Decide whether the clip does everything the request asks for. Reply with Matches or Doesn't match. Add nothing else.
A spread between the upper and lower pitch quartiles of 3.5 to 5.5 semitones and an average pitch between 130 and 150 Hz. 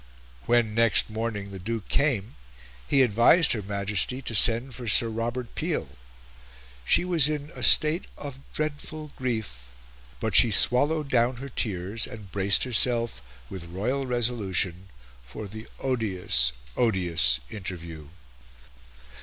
Doesn't match